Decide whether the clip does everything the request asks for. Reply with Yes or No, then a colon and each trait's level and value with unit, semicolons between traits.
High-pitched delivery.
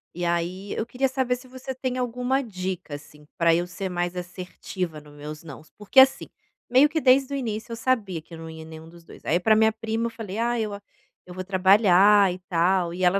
Yes: high, 195 Hz